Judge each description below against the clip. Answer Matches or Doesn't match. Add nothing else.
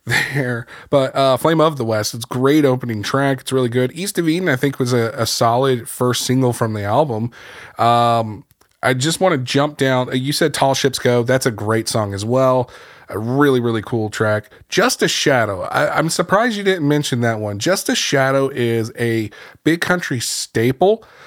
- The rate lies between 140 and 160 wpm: Doesn't match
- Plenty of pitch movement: Doesn't match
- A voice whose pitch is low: Matches